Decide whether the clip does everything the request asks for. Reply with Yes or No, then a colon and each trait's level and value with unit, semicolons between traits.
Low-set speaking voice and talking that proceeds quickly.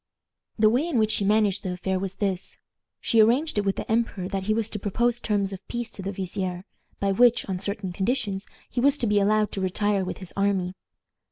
No: high, 200 Hz; fast, 225 wpm